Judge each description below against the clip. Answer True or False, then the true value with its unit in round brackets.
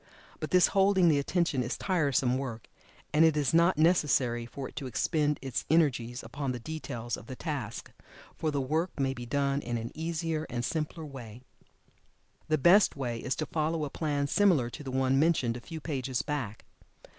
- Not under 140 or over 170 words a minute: False (190 wpm)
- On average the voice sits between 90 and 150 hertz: True (140 Hz)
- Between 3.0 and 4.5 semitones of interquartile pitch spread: True (4.2 semitones)